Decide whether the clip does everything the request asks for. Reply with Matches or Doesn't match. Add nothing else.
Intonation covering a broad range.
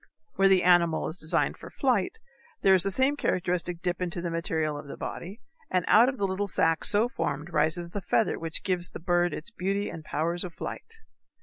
Doesn't match